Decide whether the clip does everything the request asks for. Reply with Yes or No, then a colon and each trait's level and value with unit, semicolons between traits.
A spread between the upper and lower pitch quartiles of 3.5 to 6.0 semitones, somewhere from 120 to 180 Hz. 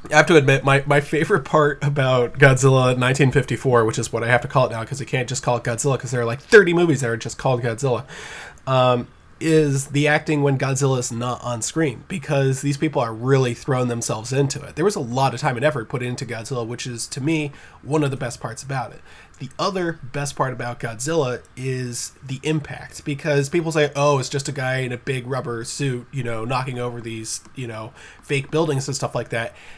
No: average, 3.0 semitones; low, 135 Hz